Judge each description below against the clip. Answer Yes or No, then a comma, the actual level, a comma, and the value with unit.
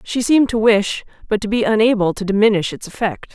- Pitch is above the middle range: Yes, high, 215 Hz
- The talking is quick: Yes, fast, 215 wpm